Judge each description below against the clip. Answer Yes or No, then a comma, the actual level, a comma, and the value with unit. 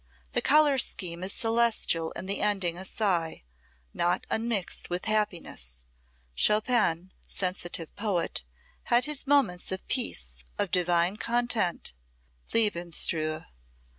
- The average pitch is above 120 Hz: Yes, medium, 185 Hz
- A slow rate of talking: Yes, slow, 110 wpm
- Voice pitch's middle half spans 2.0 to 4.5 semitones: No, average, 4.9 semitones